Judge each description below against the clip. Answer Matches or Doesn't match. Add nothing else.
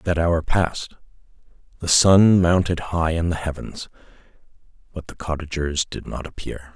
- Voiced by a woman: Doesn't match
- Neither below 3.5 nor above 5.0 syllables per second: Matches